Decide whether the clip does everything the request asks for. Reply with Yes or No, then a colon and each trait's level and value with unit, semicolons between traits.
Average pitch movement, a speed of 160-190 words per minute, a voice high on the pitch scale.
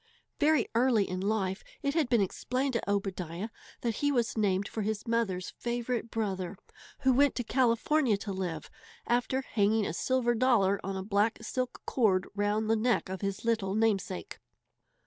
Yes: average, 3.7 semitones; average, 165 wpm; high, 220 Hz